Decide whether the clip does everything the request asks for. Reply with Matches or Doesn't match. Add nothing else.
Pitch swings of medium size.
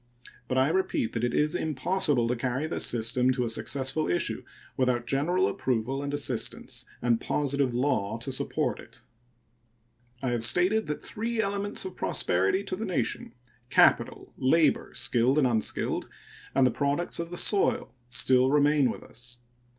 Matches